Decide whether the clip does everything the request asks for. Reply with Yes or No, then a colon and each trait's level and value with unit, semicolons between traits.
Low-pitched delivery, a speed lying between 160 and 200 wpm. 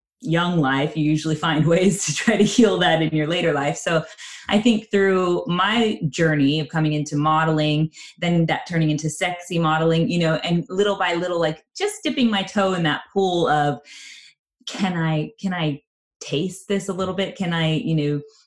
No: medium, 165 Hz; average, 190 wpm